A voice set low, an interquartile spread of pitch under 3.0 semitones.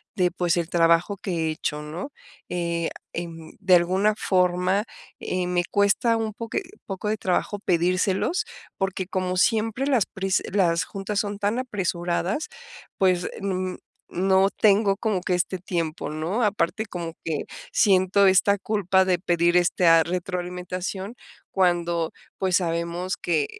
No: medium, 185 Hz; narrow, 2.6 semitones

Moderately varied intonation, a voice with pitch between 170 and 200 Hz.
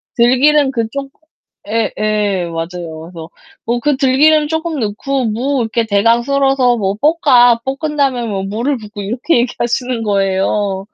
No: average, 4.9 semitones; high, 235 Hz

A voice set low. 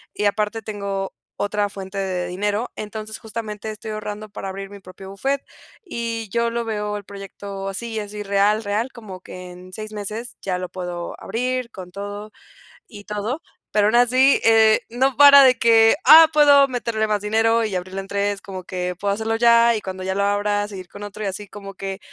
No: high, 210 Hz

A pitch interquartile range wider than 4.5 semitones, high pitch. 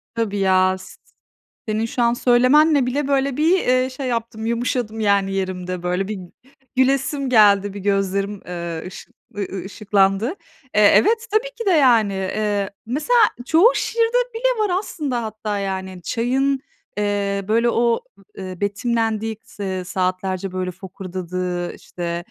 Yes: average, 5.1 semitones; high, 215 Hz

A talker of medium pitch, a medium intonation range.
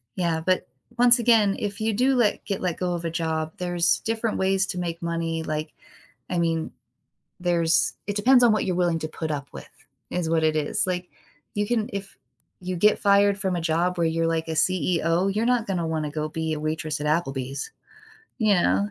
Yes: medium, 175 Hz; average, 3.8 semitones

